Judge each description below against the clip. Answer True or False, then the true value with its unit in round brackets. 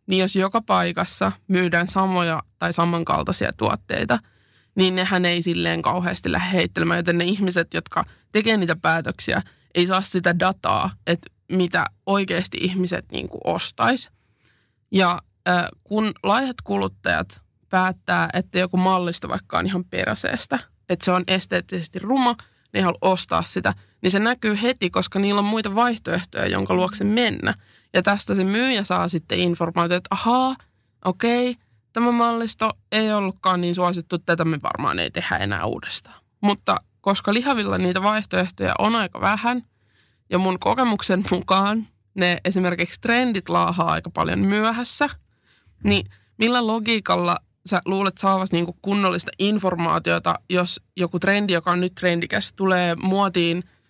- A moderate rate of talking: True (140 wpm)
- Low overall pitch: False (185 Hz)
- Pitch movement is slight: False (3.1 semitones)